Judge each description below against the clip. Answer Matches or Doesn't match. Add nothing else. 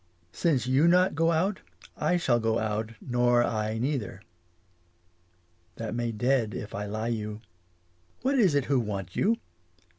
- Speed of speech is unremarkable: Matches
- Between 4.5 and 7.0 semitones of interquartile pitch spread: Matches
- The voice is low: Matches